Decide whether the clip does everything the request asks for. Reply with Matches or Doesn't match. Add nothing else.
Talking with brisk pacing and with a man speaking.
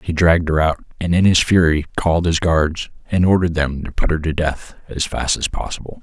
Matches